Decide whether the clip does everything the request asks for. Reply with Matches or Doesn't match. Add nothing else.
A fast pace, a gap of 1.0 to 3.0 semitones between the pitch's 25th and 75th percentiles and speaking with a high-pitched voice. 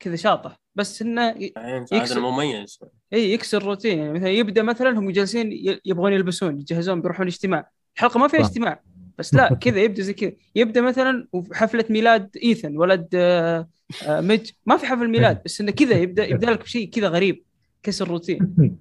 Doesn't match